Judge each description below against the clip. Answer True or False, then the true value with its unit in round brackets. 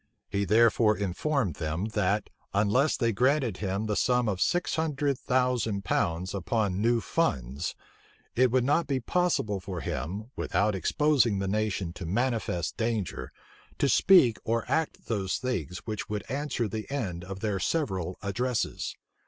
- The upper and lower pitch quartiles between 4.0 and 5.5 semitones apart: True (4.9 semitones)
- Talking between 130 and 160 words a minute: True (150 wpm)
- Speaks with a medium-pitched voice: False (110 Hz)